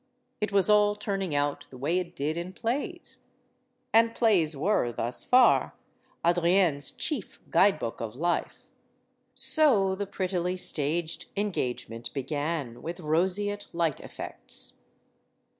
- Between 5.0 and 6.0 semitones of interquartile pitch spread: Yes, wide, 5.5 semitones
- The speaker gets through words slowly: Yes, slow, 125 wpm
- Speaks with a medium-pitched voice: Yes, medium, 175 Hz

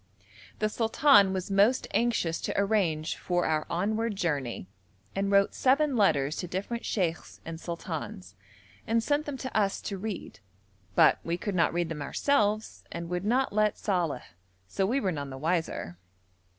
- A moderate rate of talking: Yes, average, 165 wpm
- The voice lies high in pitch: Yes, high, 195 Hz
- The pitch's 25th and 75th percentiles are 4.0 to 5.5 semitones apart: Yes, average, 4.8 semitones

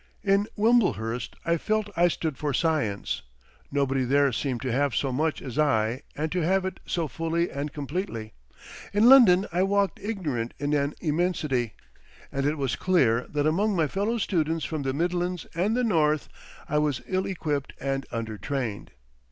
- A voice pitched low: No, medium, 155 Hz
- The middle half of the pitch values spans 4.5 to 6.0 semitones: Yes, average, 5.1 semitones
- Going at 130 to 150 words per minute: No, average, 170 wpm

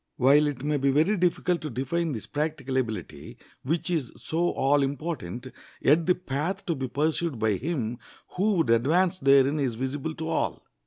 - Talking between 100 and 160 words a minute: No, average, 175 wpm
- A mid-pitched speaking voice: Yes, medium, 145 Hz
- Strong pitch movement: No, average, 4.1 semitones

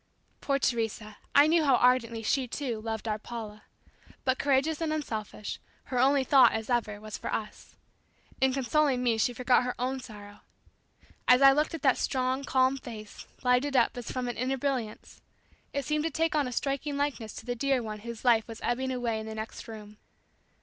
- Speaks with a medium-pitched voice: No, very high, 250 Hz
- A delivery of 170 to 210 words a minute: Yes, average, 195 wpm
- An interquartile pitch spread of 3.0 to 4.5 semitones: Yes, average, 3.4 semitones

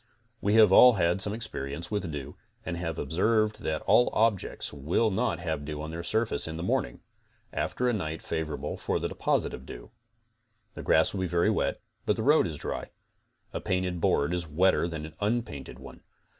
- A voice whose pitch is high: No, very low, 85 Hz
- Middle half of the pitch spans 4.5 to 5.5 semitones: Yes, average, 5.0 semitones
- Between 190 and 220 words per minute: Yes, average, 200 wpm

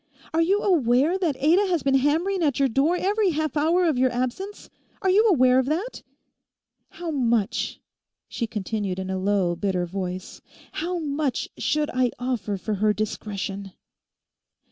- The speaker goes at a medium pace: Yes, average, 160 wpm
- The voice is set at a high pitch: Yes, very high, 270 Hz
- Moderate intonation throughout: No, wide, 8.1 semitones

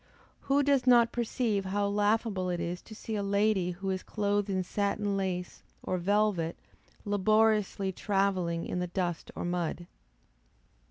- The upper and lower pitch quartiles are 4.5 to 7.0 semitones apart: No, average, 2.9 semitones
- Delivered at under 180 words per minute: Yes, average, 150 wpm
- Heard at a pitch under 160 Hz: No, high, 200 Hz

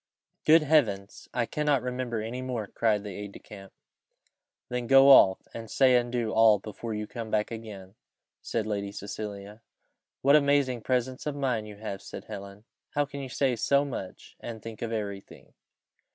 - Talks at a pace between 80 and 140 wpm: No, average, 180 wpm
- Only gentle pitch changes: No, average, 3.7 semitones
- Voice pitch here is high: No, low, 115 Hz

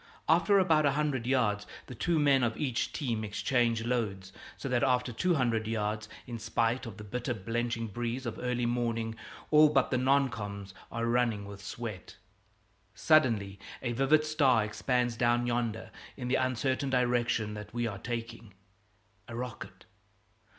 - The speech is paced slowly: No, average, 160 wpm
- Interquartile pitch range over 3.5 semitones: No, average, 2.7 semitones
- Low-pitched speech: Yes, low, 120 Hz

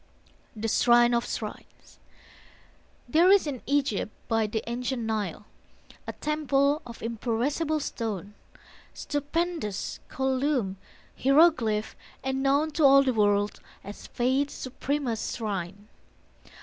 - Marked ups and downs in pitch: No, average, 4.7 semitones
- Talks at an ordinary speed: No, slow, 110 wpm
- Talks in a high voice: Yes, very high, 250 Hz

